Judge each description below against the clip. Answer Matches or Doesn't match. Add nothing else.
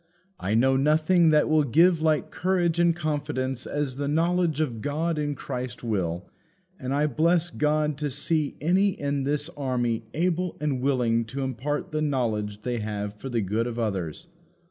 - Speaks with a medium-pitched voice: Matches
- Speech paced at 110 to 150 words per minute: Doesn't match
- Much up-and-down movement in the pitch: Doesn't match